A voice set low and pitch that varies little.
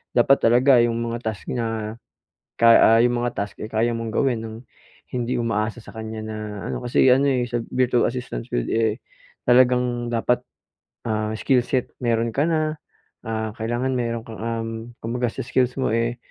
Yes: low, 120 Hz; narrow, 1.7 semitones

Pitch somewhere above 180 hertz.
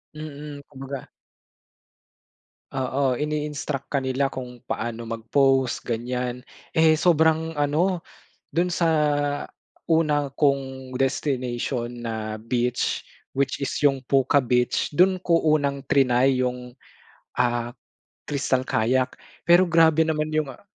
No: low, 135 Hz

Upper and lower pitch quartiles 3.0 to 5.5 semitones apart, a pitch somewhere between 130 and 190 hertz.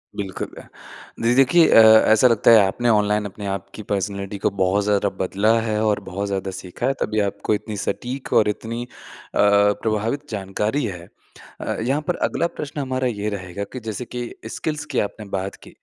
No: average, 3.4 semitones; low, 105 Hz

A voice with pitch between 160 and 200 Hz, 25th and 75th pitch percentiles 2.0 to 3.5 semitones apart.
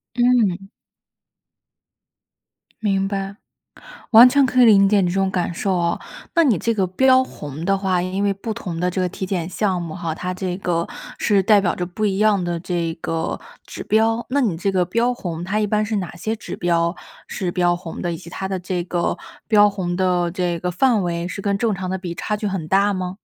Yes: high, 190 Hz; average, 2.9 semitones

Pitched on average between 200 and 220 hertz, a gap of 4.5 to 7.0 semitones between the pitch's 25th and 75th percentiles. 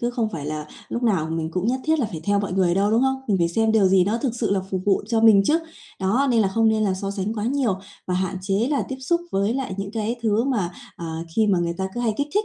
No: high, 210 Hz; average, 4.0 semitones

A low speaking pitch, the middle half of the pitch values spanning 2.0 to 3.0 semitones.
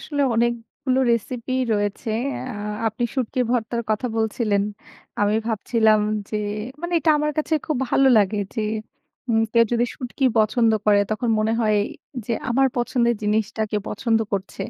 No: high, 230 Hz; average, 2.7 semitones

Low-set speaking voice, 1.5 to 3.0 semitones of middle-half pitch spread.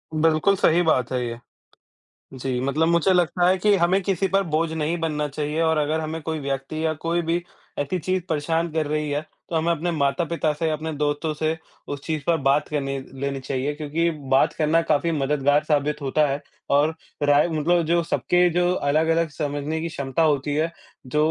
No: medium, 155 Hz; narrow, 2.4 semitones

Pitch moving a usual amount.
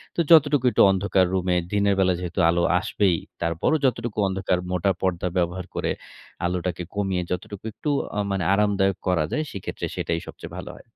No: narrow, 2.3 semitones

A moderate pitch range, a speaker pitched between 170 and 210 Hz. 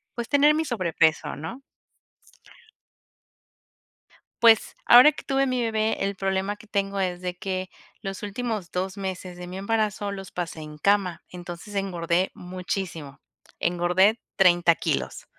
Yes: average, 3.2 semitones; high, 190 Hz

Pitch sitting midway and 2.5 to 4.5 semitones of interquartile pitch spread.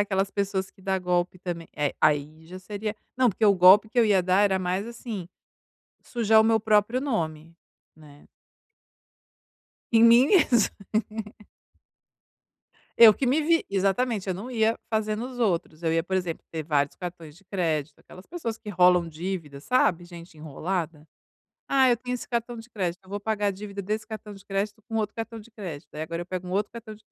No: high, 195 Hz; average, 4.2 semitones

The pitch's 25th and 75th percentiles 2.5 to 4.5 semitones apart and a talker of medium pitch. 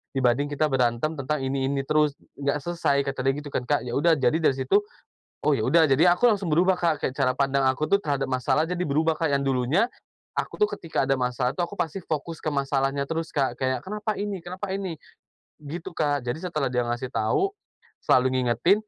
Yes: average, 4.0 semitones; medium, 145 Hz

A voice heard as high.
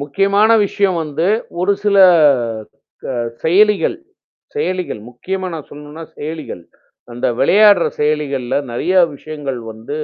No: medium, 160 Hz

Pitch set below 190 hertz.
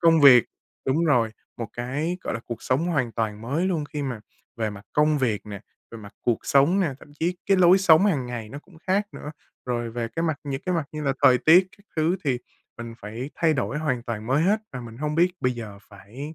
Yes: medium, 140 Hz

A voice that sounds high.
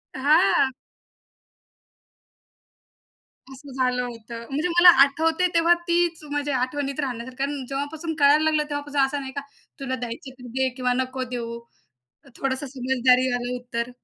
Yes: very high, 270 Hz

